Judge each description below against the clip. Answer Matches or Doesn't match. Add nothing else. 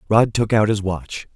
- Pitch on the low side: Matches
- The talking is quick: Matches